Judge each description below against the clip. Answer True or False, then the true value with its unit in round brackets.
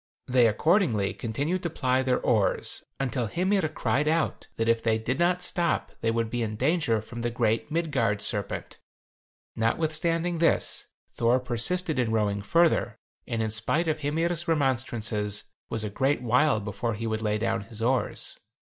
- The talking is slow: False (165 wpm)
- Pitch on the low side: True (125 Hz)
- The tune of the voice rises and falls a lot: True (6.0 semitones)